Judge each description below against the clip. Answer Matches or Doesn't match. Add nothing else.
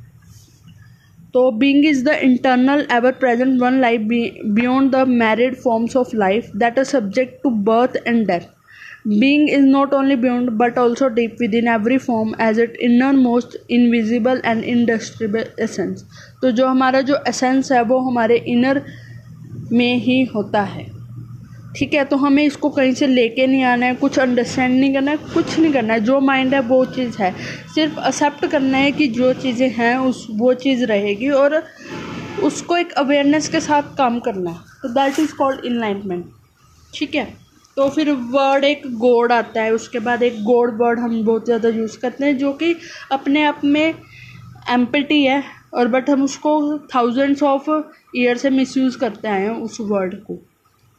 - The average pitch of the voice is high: Matches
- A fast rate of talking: Doesn't match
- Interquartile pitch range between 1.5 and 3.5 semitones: Matches